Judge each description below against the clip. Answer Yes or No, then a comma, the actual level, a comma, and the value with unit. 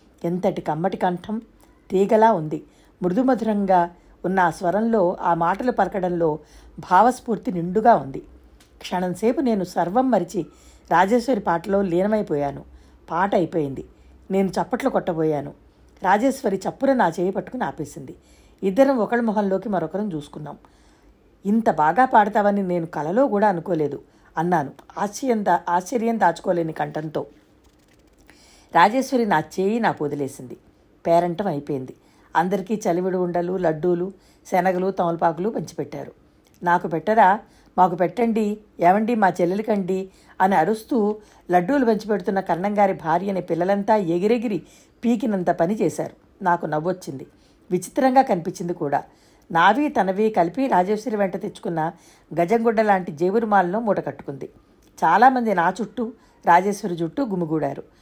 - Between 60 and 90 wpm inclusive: No, average, 105 wpm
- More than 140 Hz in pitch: Yes, high, 190 Hz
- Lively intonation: No, average, 4.1 semitones